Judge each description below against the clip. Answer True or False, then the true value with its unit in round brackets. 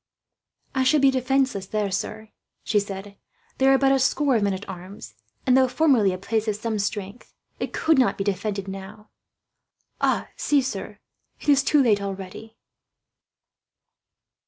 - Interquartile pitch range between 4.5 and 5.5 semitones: True (5.0 semitones)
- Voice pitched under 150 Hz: False (215 Hz)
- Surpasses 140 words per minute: True (160 wpm)